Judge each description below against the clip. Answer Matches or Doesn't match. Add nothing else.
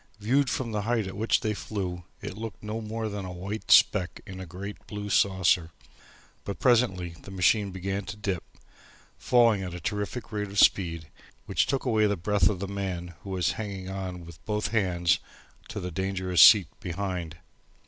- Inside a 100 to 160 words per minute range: Doesn't match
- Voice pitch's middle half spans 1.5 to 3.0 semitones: Matches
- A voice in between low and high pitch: Doesn't match